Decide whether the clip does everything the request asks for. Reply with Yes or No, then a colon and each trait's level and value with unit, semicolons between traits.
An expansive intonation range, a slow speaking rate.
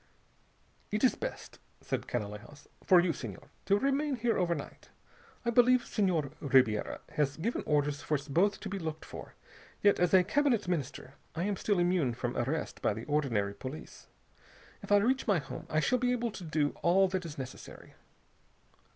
No: wide, 6.3 semitones; average, 175 wpm